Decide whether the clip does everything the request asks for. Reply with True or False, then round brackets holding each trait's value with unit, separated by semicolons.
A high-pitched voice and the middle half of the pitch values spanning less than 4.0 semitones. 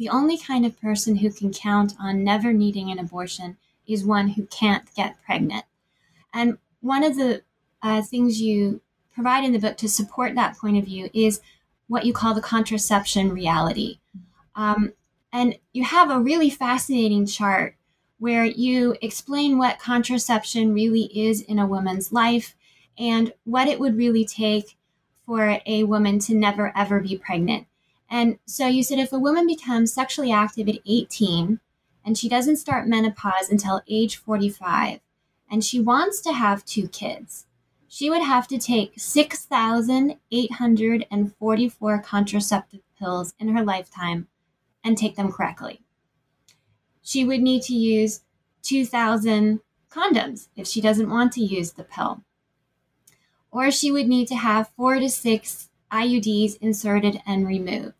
True (220 Hz; 3.1 semitones)